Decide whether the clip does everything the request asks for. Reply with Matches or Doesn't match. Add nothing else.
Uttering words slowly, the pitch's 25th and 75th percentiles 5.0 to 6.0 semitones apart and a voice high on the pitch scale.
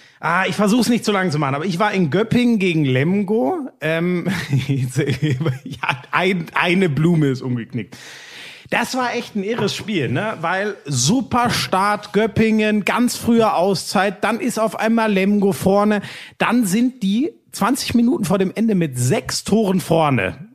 Doesn't match